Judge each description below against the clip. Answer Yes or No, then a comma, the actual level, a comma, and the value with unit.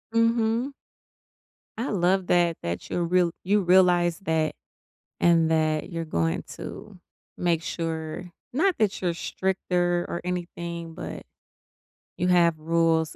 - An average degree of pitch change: No, narrow, 2.2 semitones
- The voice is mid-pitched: Yes, medium, 175 Hz